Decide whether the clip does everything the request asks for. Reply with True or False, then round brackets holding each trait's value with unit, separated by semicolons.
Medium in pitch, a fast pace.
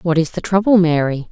True (170 Hz; 230 wpm)